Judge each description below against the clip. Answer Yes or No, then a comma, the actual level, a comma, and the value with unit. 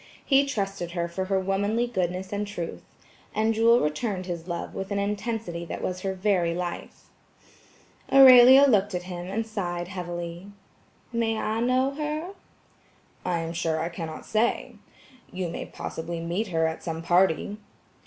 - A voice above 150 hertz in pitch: Yes, high, 190 Hz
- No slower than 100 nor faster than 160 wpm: Yes, average, 155 wpm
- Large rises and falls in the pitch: No, average, 4.3 semitones